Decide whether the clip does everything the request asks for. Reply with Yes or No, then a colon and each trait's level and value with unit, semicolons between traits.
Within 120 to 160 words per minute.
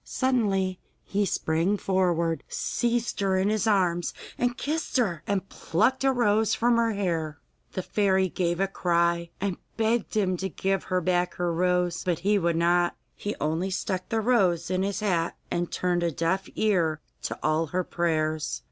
No: average, 175 wpm